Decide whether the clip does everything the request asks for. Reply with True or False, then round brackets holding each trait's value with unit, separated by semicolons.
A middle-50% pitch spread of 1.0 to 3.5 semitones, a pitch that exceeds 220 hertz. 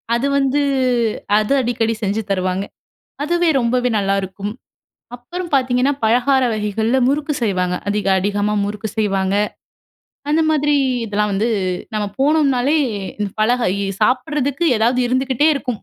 False (4.8 semitones; 240 Hz)